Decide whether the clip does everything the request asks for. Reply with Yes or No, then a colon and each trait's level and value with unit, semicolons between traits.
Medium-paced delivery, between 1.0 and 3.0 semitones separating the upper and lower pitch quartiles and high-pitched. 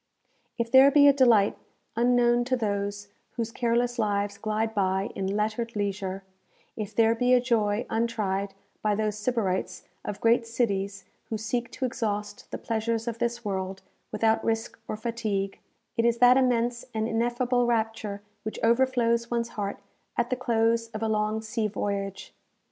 Yes: average, 160 wpm; narrow, 2.5 semitones; high, 225 Hz